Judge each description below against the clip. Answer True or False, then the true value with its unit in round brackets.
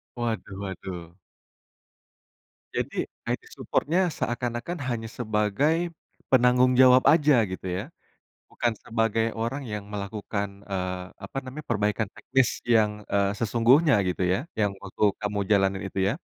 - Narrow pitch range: False (4.1 semitones)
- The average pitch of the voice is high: False (110 Hz)